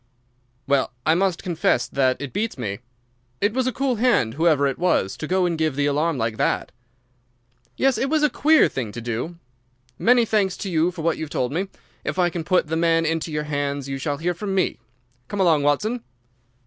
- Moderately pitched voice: Yes, medium, 165 Hz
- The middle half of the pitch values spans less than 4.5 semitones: No, average, 5.3 semitones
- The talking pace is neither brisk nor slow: No, fast, 210 wpm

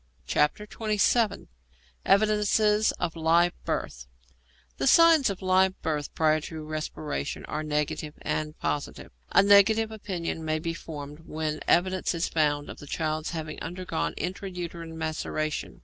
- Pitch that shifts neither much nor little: Yes, average, 4.1 semitones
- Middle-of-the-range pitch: Yes, medium, 165 Hz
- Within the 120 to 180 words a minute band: Yes, slow, 135 wpm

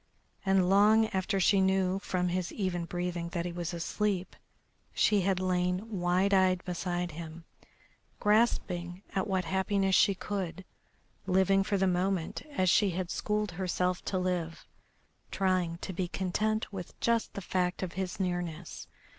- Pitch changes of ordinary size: No, narrow, 1.7 semitones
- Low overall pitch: No, medium, 185 Hz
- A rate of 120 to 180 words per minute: Yes, average, 150 wpm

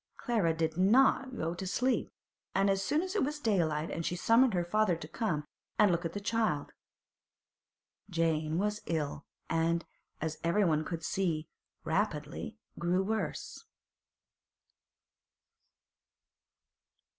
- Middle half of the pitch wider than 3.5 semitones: Yes, average, 4.9 semitones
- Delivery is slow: Yes, slow, 120 wpm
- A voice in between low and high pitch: Yes, medium, 175 Hz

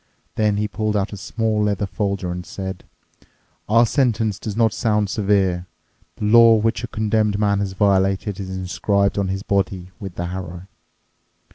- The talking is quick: No, average, 165 wpm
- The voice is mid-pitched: No, low, 100 Hz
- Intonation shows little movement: Yes, narrow, 2.1 semitones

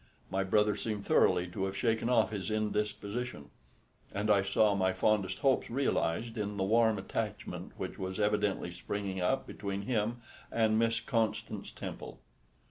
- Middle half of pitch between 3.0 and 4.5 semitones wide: No, narrow, 2.5 semitones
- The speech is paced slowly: No, average, 150 wpm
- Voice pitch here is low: Yes, low, 105 Hz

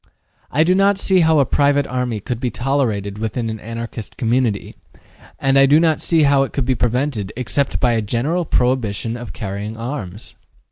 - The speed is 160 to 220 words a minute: Yes, average, 185 wpm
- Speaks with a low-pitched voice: Yes, low, 125 Hz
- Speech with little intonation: No, average, 4.1 semitones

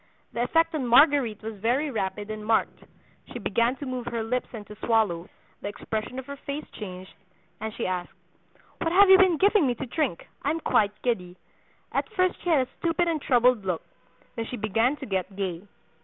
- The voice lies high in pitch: Yes, high, 235 Hz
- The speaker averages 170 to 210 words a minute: Yes, average, 200 wpm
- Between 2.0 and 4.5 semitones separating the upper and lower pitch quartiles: No, wide, 5.6 semitones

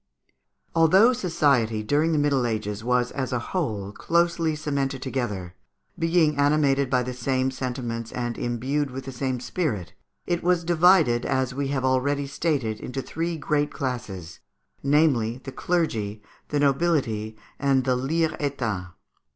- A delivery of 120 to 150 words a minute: Yes, average, 145 wpm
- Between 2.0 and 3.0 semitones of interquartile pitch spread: No, average, 4.1 semitones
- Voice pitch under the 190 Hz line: Yes, low, 135 Hz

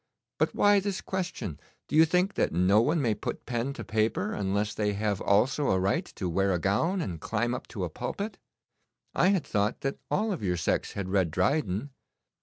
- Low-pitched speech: Yes, low, 105 Hz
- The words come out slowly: No, fast, 205 wpm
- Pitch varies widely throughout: Yes, wide, 8.4 semitones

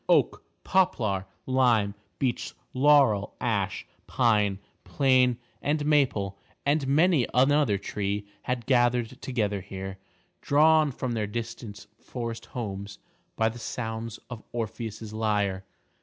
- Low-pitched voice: Yes, low, 115 Hz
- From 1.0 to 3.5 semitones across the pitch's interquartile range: No, average, 4.2 semitones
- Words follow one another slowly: Yes, slow, 110 wpm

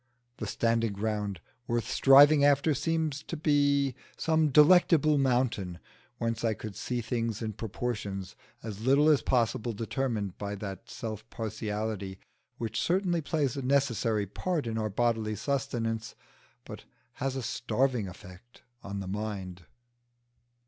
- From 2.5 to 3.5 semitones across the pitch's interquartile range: No, average, 4.7 semitones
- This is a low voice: Yes, low, 115 Hz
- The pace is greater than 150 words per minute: No, slow, 135 wpm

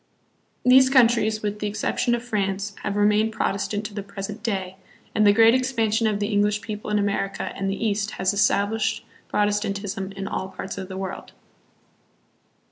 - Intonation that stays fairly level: Yes, narrow, 1.8 semitones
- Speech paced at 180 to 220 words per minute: No, average, 170 wpm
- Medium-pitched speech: No, high, 210 Hz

